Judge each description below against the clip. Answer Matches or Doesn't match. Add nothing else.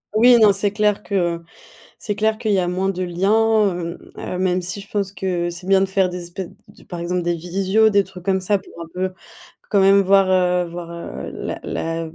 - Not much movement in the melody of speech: Matches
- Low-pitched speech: Doesn't match